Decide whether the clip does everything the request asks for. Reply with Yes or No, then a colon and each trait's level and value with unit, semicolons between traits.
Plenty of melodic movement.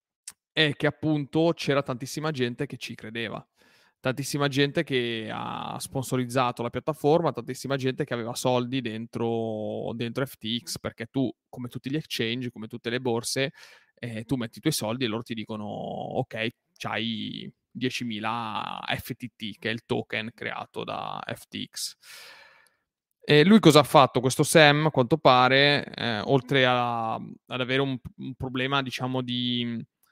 No: average, 3.2 semitones